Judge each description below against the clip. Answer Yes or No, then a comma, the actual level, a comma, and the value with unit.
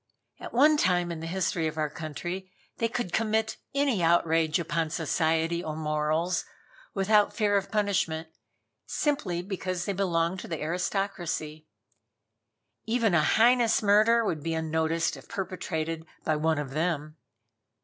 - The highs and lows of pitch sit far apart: No, average, 4.1 semitones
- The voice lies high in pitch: No, medium, 175 Hz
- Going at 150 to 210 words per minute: No, average, 140 wpm